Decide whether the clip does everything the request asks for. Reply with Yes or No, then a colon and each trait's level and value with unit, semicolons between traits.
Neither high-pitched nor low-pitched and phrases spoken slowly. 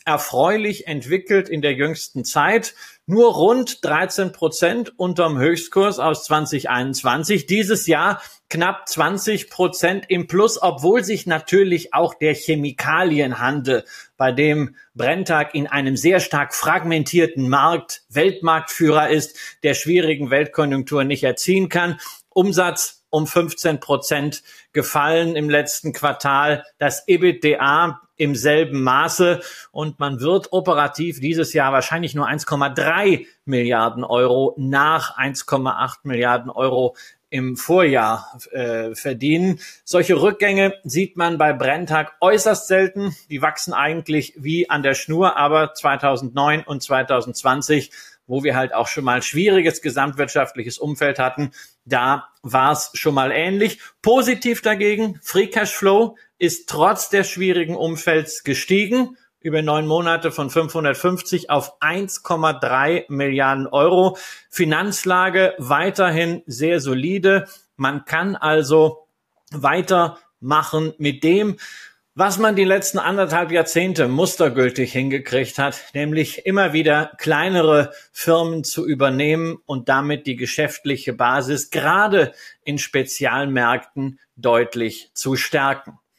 Yes: medium, 155 Hz; slow, 115 wpm